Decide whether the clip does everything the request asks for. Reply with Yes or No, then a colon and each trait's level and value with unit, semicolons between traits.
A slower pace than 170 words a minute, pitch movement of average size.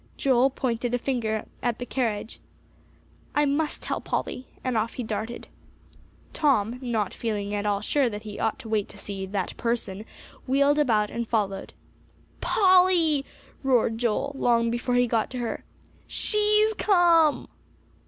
Yes: average, 150 wpm; average, 4.3 semitones